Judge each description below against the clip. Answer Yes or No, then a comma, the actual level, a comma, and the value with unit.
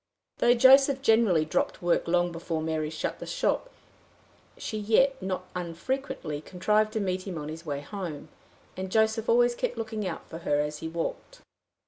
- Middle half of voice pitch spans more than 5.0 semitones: Yes, wide, 5.6 semitones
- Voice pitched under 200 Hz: Yes, medium, 185 Hz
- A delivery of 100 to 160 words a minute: No, average, 170 wpm